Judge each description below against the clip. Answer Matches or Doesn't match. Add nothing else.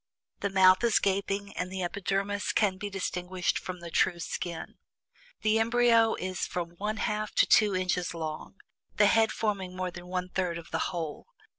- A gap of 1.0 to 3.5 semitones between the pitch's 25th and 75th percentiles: Matches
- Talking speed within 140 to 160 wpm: Doesn't match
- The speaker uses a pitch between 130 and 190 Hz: Matches